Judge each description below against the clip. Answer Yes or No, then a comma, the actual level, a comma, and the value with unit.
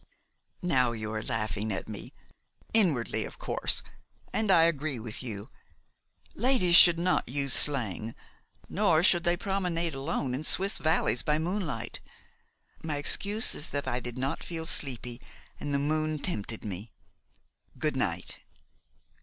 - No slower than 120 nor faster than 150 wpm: Yes, average, 140 wpm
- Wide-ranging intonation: Yes, wide, 6.4 semitones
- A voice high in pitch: No, medium, 145 Hz